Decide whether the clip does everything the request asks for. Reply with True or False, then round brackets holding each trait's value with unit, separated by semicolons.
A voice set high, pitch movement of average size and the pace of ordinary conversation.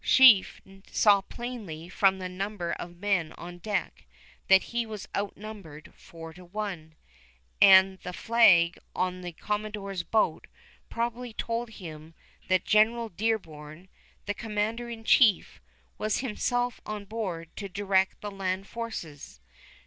False (200 Hz; 3.8 semitones; 130 wpm)